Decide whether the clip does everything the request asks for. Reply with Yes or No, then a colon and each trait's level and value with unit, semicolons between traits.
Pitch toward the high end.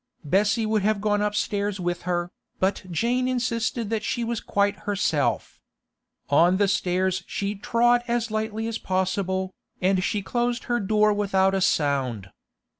Yes: high, 205 Hz